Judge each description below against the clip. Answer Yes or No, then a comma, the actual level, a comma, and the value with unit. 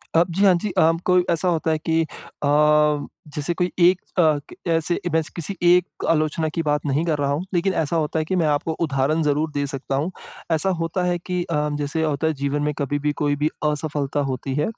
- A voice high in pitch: No, medium, 155 Hz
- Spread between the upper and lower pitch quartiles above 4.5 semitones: No, average, 2.7 semitones